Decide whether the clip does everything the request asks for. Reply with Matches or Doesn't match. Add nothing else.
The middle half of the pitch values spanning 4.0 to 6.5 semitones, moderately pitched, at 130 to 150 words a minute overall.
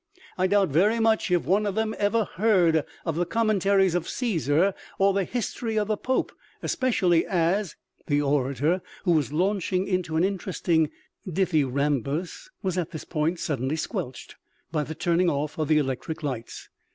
Doesn't match